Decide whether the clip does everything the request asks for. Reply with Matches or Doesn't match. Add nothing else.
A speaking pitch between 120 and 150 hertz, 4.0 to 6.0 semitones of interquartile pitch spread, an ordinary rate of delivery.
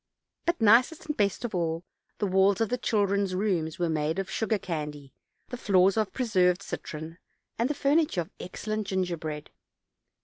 Doesn't match